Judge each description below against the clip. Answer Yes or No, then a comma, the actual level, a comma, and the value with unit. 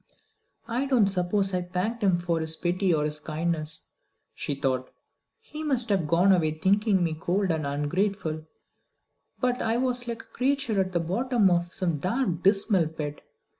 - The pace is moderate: Yes, average, 170 wpm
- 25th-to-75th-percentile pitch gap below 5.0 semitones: No, wide, 5.4 semitones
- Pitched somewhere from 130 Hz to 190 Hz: Yes, medium, 185 Hz